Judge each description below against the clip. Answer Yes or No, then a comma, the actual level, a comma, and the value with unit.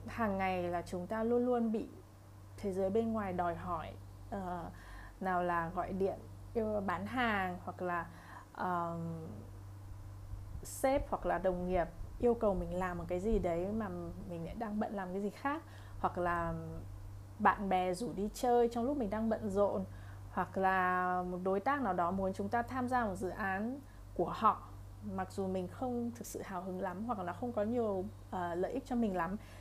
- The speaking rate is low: No, average, 195 wpm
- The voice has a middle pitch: Yes, medium, 180 Hz